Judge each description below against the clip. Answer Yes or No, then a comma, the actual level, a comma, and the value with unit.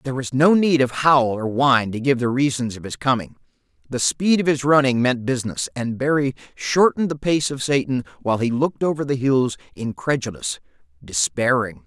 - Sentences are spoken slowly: No, average, 185 wpm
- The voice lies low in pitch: Yes, low, 130 Hz